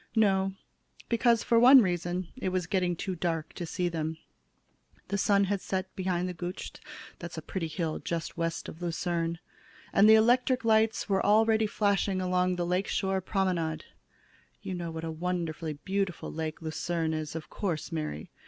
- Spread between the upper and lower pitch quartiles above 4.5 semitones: No, average, 3.2 semitones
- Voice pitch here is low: No, medium, 180 Hz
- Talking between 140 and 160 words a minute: No, average, 170 wpm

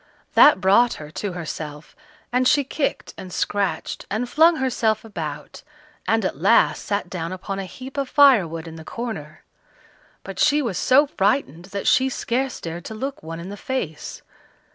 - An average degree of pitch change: No, wide, 7.4 semitones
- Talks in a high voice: Yes, high, 205 Hz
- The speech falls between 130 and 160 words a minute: No, average, 170 wpm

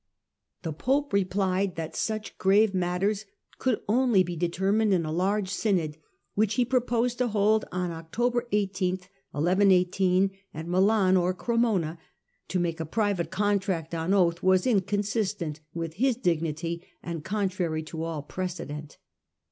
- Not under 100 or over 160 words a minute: Yes, slow, 135 wpm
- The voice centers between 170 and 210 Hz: Yes, medium, 185 Hz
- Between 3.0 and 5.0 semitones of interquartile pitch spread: Yes, average, 3.9 semitones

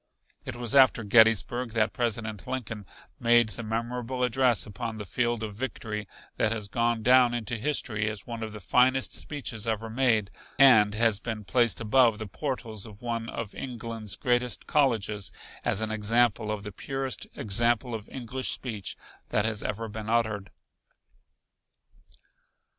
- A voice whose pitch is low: Yes, low, 115 Hz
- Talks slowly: No, average, 155 wpm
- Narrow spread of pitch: Yes, narrow, 2.3 semitones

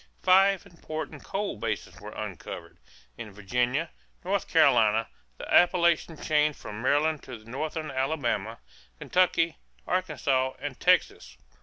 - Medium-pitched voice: Yes, medium, 145 Hz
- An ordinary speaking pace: No, slow, 115 wpm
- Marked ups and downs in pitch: Yes, wide, 6.3 semitones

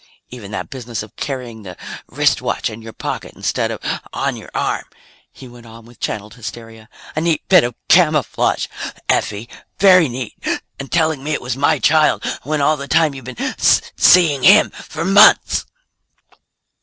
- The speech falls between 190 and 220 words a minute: No, average, 165 wpm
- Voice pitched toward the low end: Yes, low, 130 Hz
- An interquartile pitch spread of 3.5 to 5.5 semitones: Yes, average, 5.2 semitones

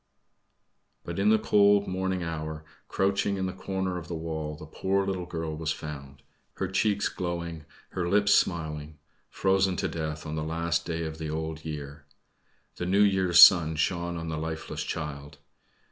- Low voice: Yes, very low, 85 Hz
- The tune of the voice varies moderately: Yes, average, 3.3 semitones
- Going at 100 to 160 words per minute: No, average, 170 wpm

